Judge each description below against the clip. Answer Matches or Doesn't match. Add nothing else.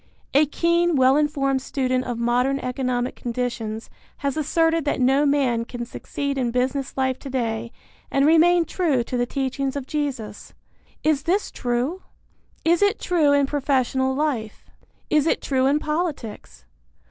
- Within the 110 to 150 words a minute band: Matches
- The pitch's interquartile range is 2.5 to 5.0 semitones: Matches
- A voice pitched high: Matches